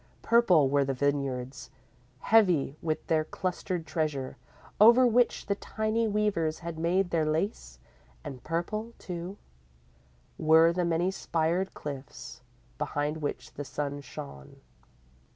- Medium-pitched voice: Yes, medium, 165 Hz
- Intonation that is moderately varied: Yes, average, 5.0 semitones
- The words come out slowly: Yes, slow, 120 wpm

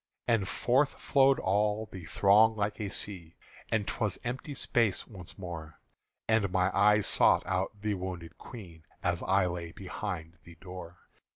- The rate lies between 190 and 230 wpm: No, average, 160 wpm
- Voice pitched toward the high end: No, low, 100 Hz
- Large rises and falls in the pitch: No, average, 3.3 semitones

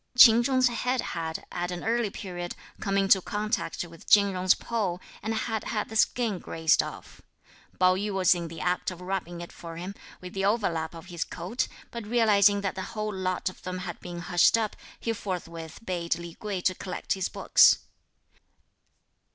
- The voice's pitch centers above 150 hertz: Yes, high, 190 Hz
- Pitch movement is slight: No, average, 3.4 semitones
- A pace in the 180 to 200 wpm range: Yes, average, 185 wpm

